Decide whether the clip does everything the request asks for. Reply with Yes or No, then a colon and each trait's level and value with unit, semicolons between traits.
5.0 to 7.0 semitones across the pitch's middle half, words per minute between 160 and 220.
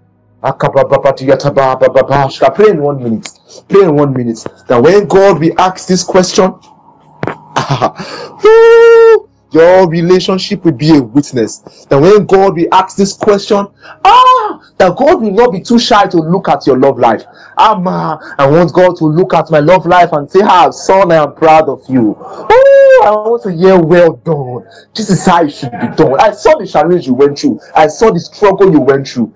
Yes: wide, 5.4 semitones; average, 180 wpm